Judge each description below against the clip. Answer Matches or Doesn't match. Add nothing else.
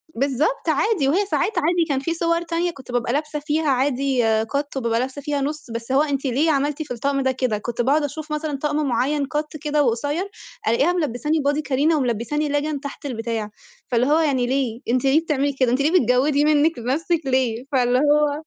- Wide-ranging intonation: Doesn't match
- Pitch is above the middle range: Matches